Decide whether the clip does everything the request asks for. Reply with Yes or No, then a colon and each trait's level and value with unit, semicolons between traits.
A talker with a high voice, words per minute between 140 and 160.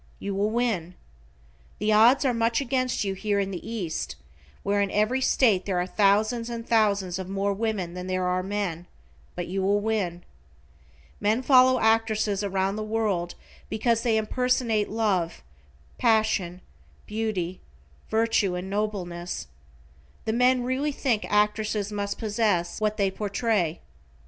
Yes: high, 210 Hz; average, 145 wpm